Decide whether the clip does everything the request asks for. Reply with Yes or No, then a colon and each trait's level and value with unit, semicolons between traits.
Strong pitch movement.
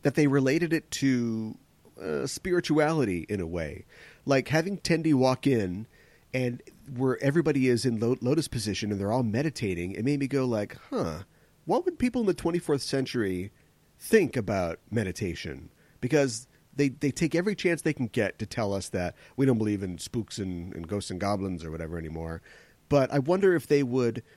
Yes: wide, 6.3 semitones